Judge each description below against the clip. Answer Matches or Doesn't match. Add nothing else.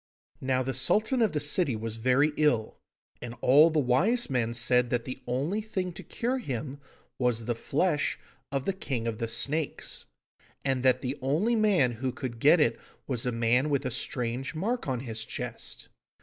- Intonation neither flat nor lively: Matches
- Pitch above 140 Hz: Doesn't match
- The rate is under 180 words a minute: Doesn't match